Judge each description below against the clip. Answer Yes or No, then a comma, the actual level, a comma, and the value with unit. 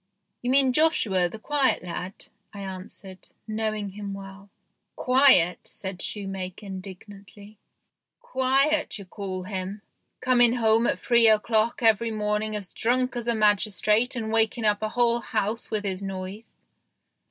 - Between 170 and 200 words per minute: No, average, 155 wpm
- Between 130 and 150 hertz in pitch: No, high, 215 Hz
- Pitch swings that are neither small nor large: Yes, average, 3.2 semitones